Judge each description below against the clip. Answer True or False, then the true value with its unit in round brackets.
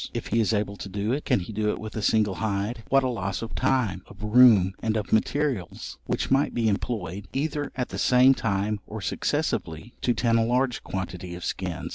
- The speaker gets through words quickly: True (215 wpm)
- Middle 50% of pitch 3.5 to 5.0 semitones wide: True (4.0 semitones)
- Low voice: True (110 Hz)